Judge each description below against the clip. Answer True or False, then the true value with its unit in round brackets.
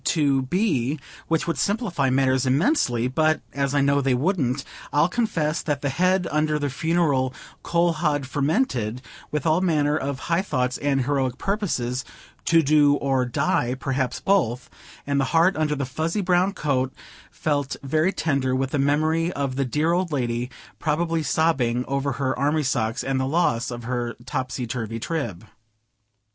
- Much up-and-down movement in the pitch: False (3.8 semitones)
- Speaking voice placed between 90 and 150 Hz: True (140 Hz)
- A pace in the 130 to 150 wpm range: False (165 wpm)